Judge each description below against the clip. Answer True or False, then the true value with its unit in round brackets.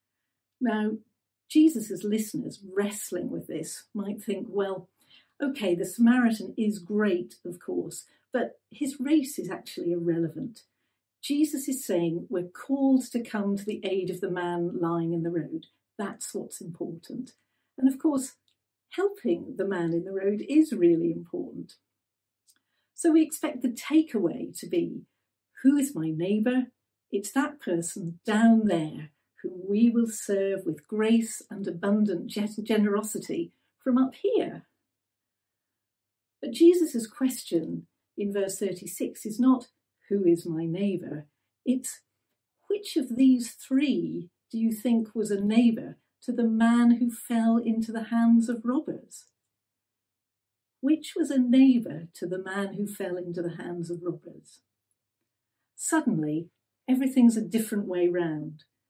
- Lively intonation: True (6.3 semitones)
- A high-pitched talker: True (210 Hz)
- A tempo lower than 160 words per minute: True (140 wpm)